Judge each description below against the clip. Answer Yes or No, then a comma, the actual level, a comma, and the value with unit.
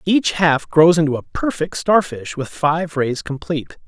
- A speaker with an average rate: Yes, average, 170 wpm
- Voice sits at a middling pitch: Yes, medium, 160 Hz